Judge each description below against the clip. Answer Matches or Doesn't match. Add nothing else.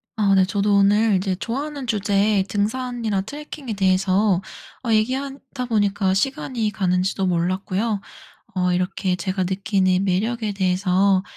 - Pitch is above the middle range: Matches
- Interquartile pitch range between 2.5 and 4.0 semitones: Matches